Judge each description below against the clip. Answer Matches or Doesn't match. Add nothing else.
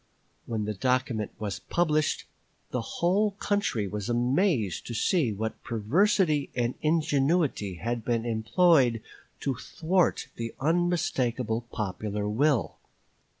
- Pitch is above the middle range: Doesn't match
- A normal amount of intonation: Doesn't match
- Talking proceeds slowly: Matches